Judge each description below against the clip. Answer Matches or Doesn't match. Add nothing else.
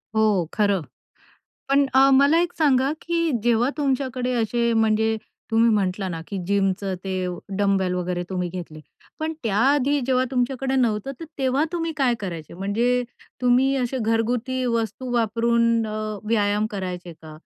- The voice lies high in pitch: Matches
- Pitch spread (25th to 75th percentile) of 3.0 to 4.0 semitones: Doesn't match